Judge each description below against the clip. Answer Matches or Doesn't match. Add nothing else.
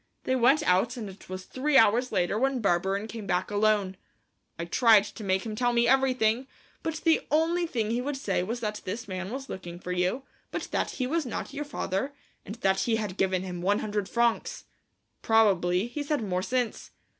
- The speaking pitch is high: Matches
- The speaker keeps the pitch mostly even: Doesn't match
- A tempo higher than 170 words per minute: Matches